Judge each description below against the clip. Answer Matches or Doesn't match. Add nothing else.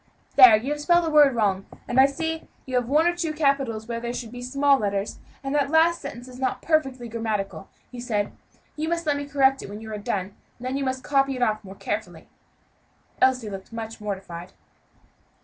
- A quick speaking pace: Matches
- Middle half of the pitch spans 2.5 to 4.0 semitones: Doesn't match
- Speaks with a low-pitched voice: Doesn't match